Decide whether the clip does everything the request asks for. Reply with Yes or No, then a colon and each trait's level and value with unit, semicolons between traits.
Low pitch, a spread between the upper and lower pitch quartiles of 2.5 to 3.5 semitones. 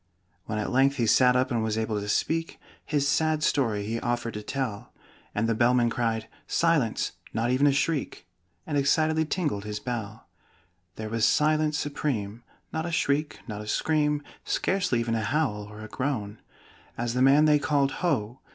No: low, 125 Hz; average, 5.1 semitones